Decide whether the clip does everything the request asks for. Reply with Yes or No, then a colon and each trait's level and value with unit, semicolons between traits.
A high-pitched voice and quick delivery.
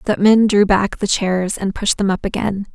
Yes: high, 200 Hz; fast, 240 wpm